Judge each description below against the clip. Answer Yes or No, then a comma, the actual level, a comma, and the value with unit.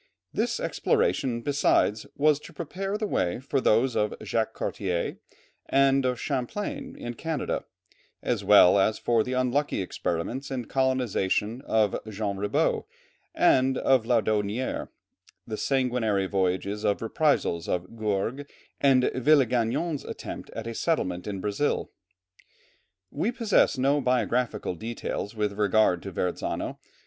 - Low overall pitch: Yes, low, 120 Hz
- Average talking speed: No, slow, 125 wpm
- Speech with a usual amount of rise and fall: Yes, average, 4.7 semitones